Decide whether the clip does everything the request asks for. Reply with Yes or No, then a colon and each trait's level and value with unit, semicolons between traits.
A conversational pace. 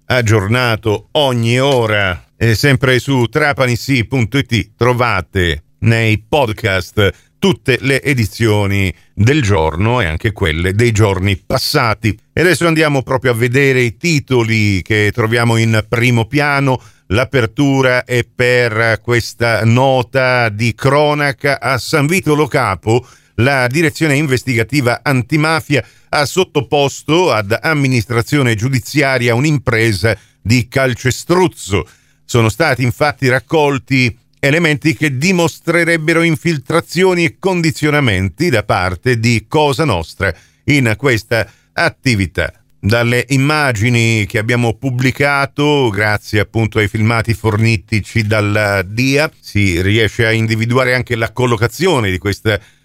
No: slow, 110 wpm